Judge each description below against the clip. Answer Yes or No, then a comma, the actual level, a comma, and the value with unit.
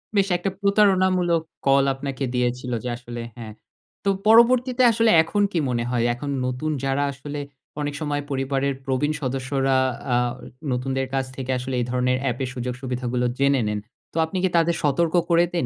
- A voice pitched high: No, low, 135 Hz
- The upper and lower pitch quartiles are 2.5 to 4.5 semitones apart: No, average, 5.0 semitones